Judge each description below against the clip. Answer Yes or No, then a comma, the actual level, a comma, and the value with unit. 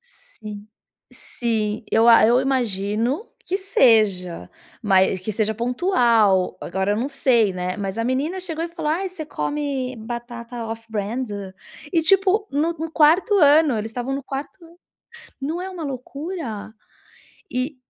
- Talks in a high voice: Yes, very high, 250 Hz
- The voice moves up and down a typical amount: No, wide, 6.4 semitones